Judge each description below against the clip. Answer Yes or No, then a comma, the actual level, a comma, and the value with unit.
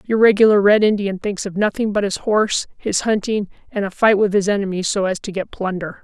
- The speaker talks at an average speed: No, fast, 230 wpm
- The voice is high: Yes, high, 200 Hz